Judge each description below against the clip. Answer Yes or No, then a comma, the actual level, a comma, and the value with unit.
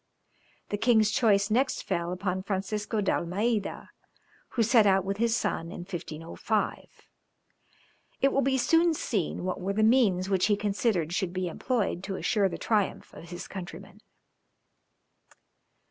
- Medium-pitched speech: No, high, 200 Hz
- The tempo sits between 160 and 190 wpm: No, average, 145 wpm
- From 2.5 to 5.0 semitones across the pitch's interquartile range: Yes, average, 3.3 semitones